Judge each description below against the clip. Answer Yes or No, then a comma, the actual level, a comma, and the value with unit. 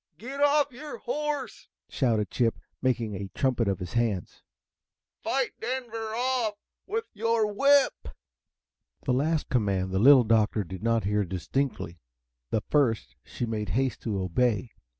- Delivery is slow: No, average, 155 wpm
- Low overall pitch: Yes, low, 125 Hz